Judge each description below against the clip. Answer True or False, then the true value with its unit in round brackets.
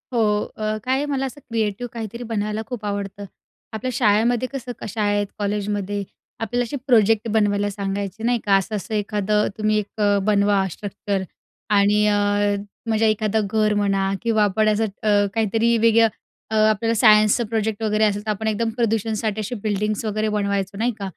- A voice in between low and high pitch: False (215 Hz)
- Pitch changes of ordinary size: False (1.7 semitones)